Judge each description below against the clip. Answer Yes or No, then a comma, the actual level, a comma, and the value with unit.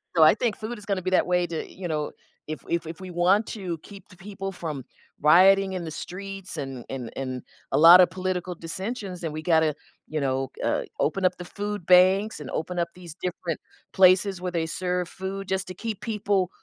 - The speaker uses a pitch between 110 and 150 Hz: No, medium, 180 Hz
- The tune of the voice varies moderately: Yes, average, 3.0 semitones